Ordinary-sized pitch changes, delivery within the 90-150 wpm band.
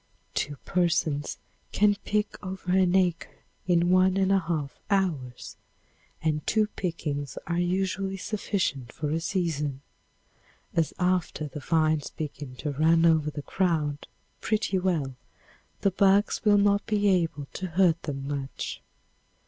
Yes: average, 4.3 semitones; slow, 135 wpm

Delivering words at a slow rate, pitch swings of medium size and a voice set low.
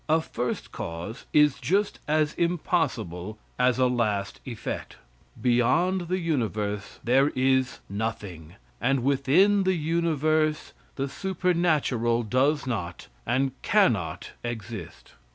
No: slow, 110 wpm; wide, 5.7 semitones; low, 130 Hz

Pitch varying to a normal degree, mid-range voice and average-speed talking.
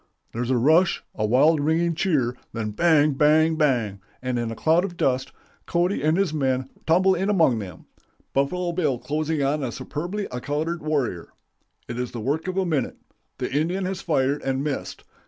Yes: average, 4.9 semitones; medium, 150 Hz; average, 185 wpm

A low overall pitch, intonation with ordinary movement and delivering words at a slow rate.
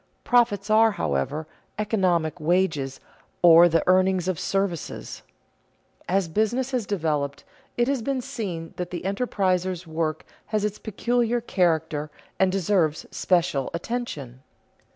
No: medium, 185 Hz; average, 4.8 semitones; slow, 120 wpm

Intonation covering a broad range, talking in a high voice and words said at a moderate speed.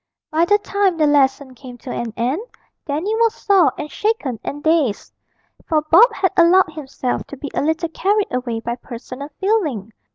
Yes: wide, 6.7 semitones; very high, 305 Hz; average, 175 wpm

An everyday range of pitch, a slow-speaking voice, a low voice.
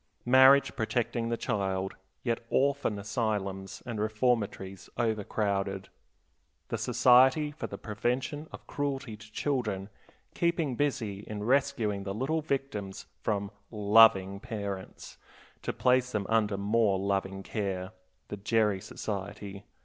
Yes: average, 4.1 semitones; slow, 120 wpm; low, 110 Hz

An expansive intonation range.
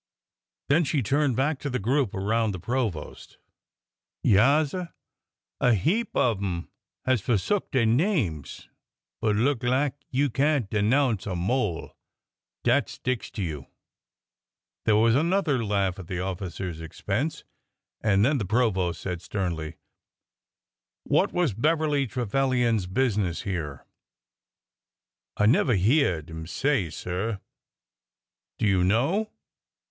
Yes: wide, 6.5 semitones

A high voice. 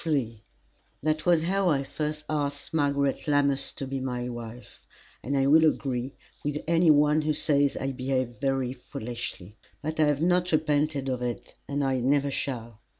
No: medium, 140 Hz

